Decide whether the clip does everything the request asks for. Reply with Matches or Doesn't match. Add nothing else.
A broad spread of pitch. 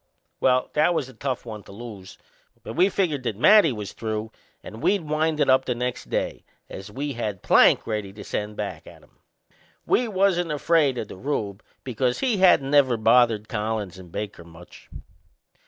Matches